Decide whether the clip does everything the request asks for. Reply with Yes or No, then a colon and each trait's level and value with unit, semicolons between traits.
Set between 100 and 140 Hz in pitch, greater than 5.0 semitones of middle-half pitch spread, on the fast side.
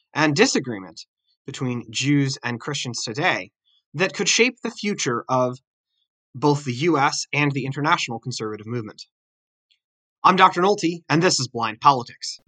No: low, 135 Hz; wide, 5.6 semitones; average, 140 wpm